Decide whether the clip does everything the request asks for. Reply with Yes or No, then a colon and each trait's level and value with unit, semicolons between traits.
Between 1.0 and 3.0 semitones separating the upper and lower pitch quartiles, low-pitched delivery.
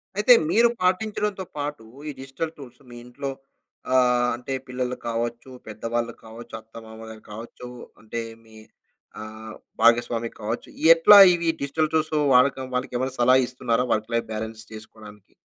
No: average, 3.7 semitones; low, 120 Hz